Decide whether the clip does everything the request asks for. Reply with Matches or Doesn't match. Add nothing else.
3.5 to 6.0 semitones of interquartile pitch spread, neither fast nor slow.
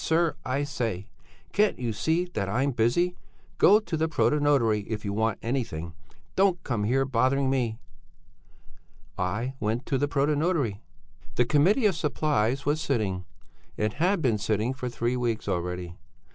Matches